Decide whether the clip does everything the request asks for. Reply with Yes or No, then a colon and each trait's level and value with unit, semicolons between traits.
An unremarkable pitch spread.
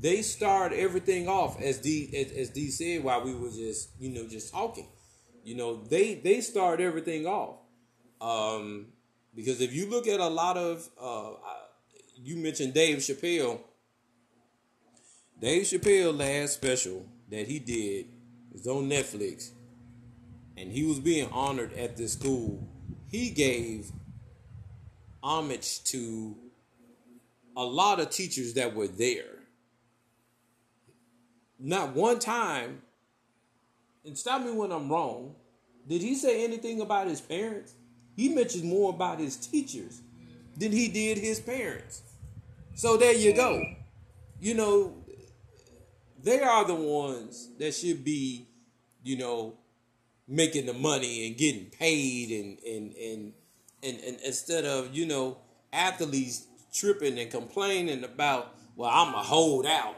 No: wide, 5.7 semitones